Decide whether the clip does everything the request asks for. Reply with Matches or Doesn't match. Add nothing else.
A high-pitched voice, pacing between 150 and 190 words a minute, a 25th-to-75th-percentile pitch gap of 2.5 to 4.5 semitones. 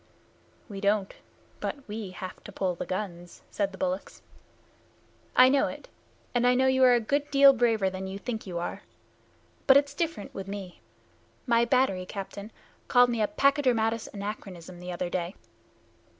Doesn't match